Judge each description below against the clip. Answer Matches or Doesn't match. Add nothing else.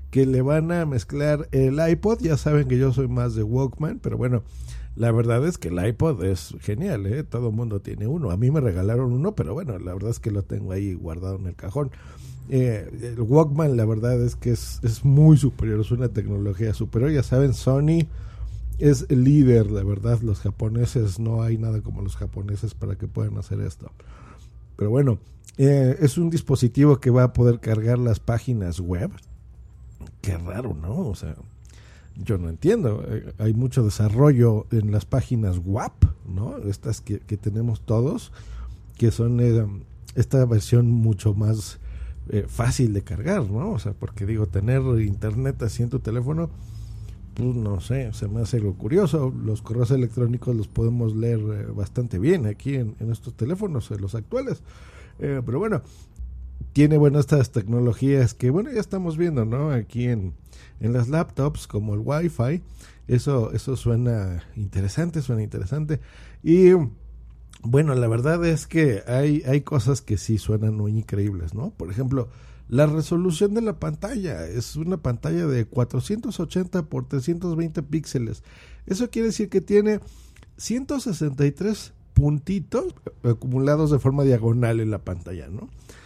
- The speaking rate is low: Doesn't match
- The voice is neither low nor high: Doesn't match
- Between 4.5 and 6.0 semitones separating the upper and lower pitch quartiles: Matches